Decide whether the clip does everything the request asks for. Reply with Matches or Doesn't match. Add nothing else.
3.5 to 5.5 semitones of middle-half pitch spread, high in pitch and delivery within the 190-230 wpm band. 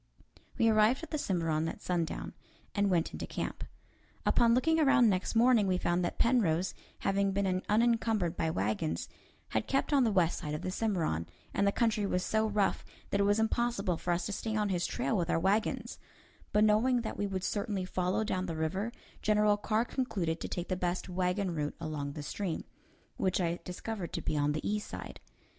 Matches